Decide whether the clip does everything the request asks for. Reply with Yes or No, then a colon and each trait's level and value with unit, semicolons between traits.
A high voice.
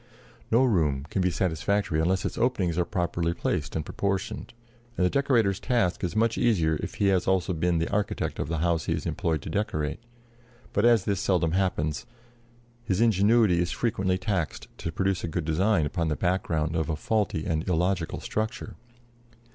No: very low, 90 Hz